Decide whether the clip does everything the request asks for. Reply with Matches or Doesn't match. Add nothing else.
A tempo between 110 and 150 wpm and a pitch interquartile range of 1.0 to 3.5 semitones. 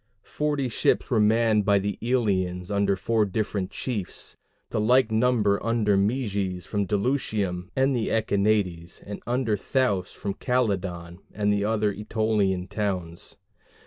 Matches